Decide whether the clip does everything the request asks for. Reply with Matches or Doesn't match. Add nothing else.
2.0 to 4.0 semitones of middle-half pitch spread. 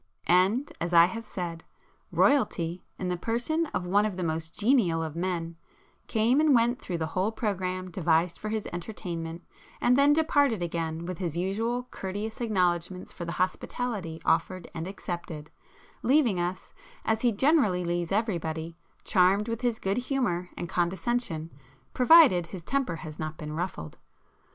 Doesn't match